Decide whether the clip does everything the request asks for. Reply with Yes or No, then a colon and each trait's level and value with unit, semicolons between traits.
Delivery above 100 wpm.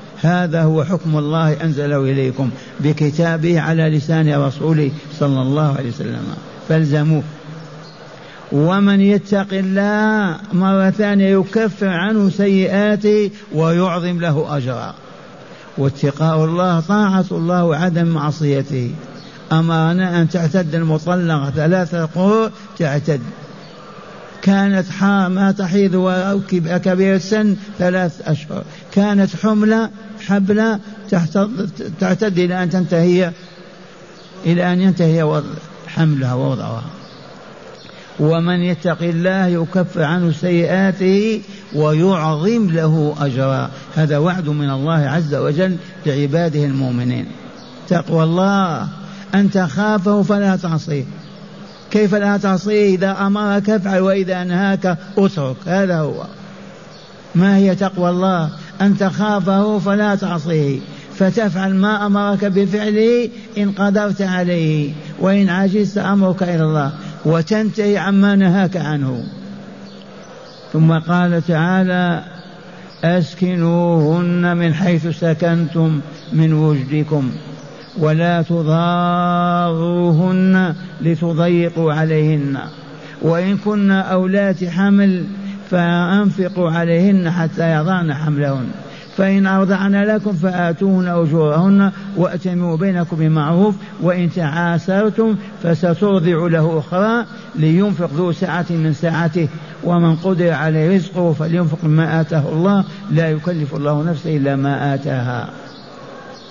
No: average, 95 wpm